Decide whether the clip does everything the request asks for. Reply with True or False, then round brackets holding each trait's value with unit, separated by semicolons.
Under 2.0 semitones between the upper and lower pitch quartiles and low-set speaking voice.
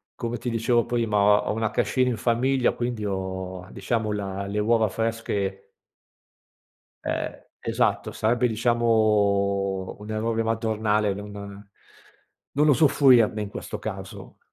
False (2.6 semitones; 110 Hz)